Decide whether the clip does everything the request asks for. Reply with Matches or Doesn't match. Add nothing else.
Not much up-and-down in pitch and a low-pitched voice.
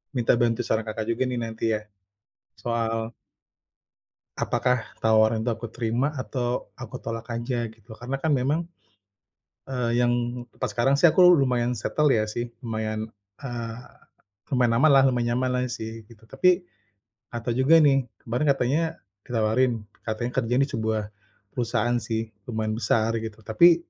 Matches